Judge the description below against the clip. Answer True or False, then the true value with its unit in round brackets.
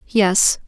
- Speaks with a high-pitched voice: True (205 Hz)